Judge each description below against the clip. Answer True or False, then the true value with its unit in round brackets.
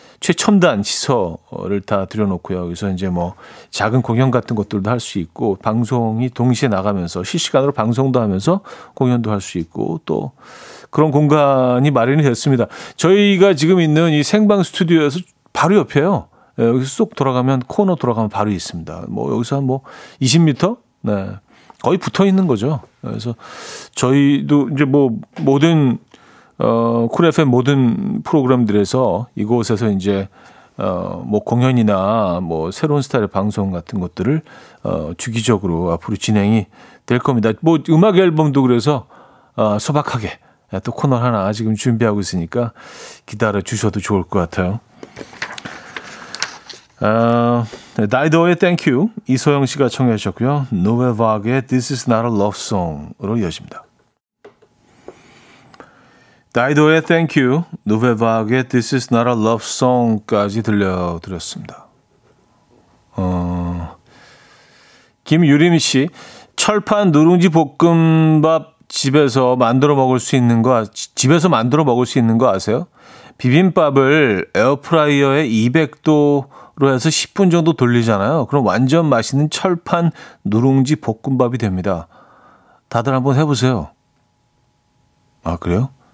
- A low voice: True (125 Hz)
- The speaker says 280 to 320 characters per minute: True (300 characters per minute)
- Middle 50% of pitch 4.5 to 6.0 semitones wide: True (5.6 semitones)